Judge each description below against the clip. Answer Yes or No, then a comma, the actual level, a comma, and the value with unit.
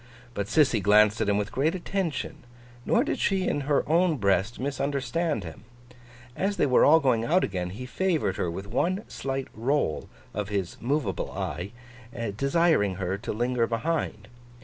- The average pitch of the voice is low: Yes, low, 125 Hz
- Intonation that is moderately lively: No, wide, 7.4 semitones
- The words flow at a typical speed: Yes, average, 165 wpm